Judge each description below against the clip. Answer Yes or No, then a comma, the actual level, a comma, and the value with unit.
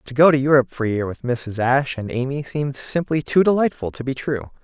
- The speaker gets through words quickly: Yes, fast, 245 wpm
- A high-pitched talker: No, low, 135 Hz